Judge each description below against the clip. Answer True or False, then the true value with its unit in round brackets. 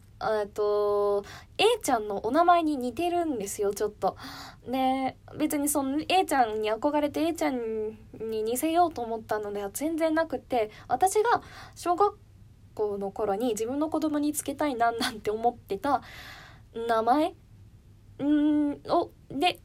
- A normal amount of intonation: False (6.6 semitones)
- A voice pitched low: False (255 Hz)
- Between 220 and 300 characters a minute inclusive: True (260 characters per minute)